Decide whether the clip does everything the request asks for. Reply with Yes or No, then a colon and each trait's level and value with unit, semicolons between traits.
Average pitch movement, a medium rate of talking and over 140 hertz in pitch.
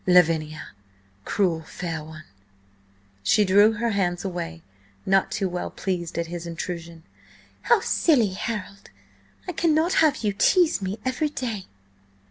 No: average, 4.8 semitones; slow, 130 wpm; high, 190 Hz